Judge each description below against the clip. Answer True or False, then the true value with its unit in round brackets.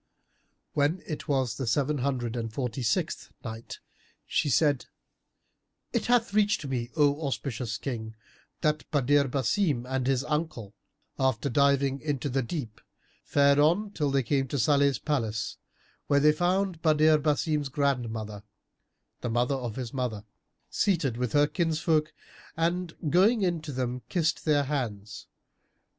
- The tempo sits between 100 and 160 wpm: True (140 wpm)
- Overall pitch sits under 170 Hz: True (140 Hz)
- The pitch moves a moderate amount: True (3.9 semitones)